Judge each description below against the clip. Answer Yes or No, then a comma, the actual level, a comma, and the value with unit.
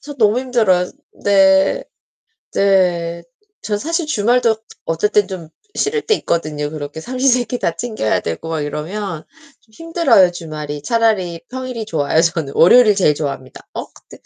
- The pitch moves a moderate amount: No, wide, 6.6 semitones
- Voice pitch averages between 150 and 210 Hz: Yes, high, 190 Hz